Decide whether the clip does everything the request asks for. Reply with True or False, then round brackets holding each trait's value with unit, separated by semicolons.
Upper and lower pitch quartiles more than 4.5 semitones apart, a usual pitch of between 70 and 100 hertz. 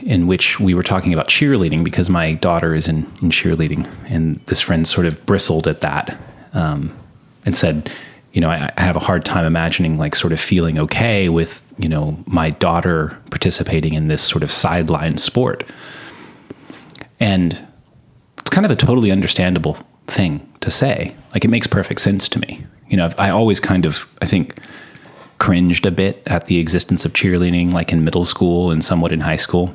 False (2.9 semitones; 85 Hz)